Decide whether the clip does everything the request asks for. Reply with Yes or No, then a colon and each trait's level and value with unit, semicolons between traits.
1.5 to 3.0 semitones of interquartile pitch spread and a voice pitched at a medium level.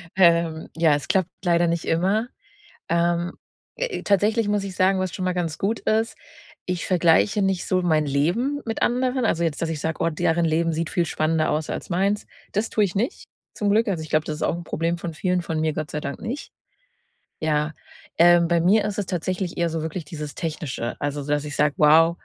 No: average, 3.6 semitones; medium, 170 Hz